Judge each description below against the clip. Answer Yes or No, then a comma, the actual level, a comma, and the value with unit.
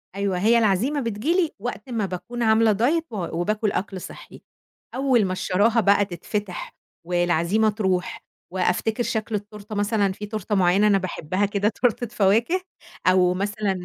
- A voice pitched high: Yes, high, 205 Hz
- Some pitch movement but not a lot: Yes, average, 3.2 semitones